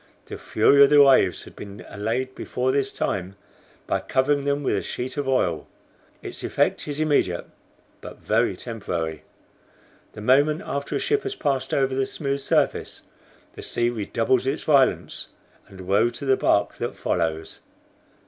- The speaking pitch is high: No, low, 130 Hz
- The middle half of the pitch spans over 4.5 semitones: Yes, wide, 5.6 semitones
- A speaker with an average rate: Yes, average, 160 wpm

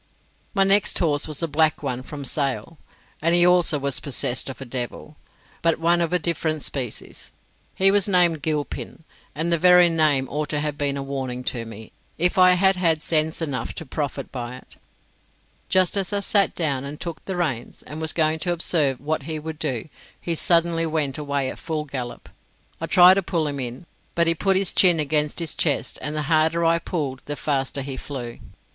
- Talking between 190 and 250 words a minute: Yes, average, 200 wpm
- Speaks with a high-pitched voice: No, medium, 155 Hz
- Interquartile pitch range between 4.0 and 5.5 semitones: No, average, 3.4 semitones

